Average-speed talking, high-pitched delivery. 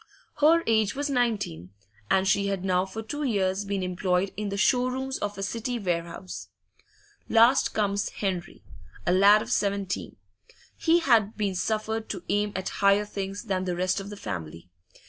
Yes: average, 170 wpm; high, 200 Hz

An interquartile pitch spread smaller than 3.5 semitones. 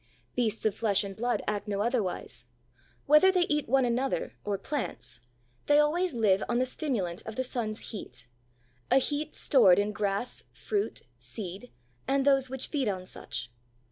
No: average, 5.1 semitones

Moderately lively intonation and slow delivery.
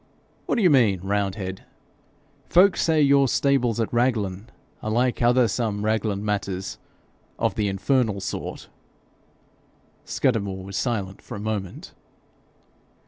Yes: average, 4.1 semitones; slow, 125 wpm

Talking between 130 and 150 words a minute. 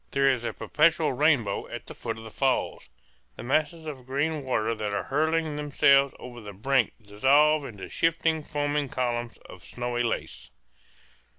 No: average, 165 wpm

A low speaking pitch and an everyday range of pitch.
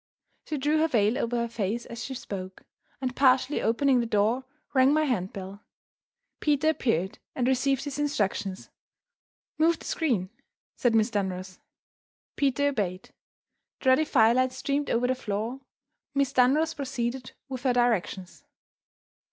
No: very high, 250 Hz; average, 4.3 semitones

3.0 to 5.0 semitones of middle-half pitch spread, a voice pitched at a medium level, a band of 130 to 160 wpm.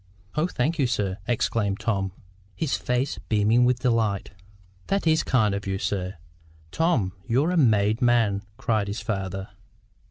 No: average, 4.0 semitones; low, 115 Hz; average, 150 wpm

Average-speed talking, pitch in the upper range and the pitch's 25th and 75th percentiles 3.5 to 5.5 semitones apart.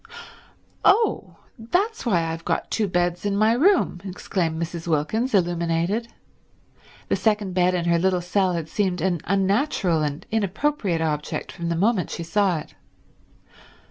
No: average, 145 wpm; medium, 180 Hz; average, 3.9 semitones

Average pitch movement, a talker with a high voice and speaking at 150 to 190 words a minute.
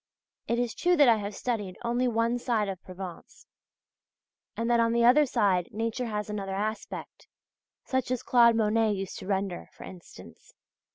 Yes: average, 3.4 semitones; high, 225 Hz; average, 170 wpm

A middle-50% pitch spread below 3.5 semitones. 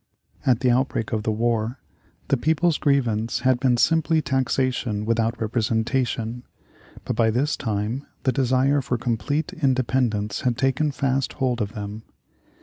Yes: average, 3.1 semitones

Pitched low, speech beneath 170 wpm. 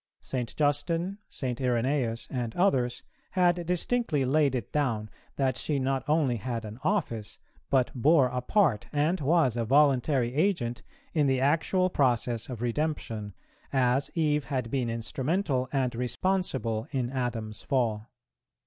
Yes: low, 130 Hz; average, 140 wpm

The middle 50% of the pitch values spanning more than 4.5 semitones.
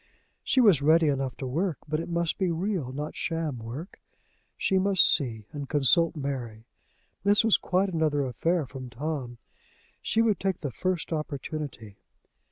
Yes: average, 5.0 semitones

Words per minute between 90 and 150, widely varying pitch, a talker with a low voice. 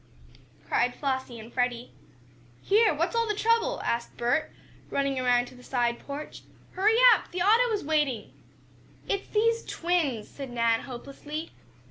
No: average, 145 wpm; wide, 8.3 semitones; very high, 280 Hz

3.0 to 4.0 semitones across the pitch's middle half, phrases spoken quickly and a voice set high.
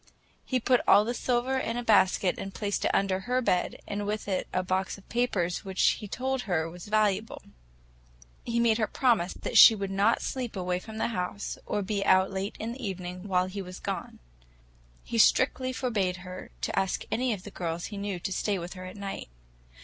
Yes: average, 3.7 semitones; fast, 210 wpm; high, 200 Hz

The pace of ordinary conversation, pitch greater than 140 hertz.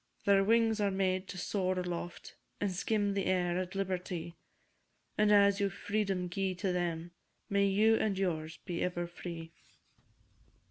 Yes: average, 150 wpm; high, 190 Hz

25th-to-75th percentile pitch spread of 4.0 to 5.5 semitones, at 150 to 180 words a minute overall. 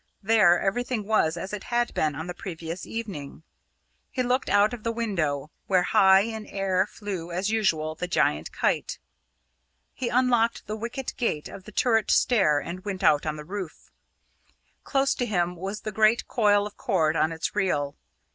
Yes: average, 4.7 semitones; average, 175 wpm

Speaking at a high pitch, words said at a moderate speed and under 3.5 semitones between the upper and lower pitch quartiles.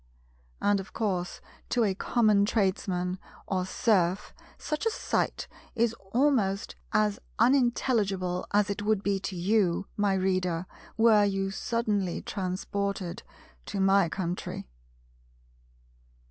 No: high, 200 Hz; slow, 115 wpm; narrow, 2.5 semitones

